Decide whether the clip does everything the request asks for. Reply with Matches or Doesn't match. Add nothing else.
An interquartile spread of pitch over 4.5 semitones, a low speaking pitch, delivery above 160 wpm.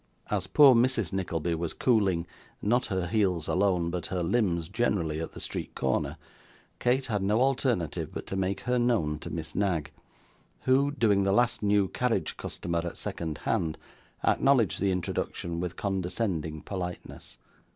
Doesn't match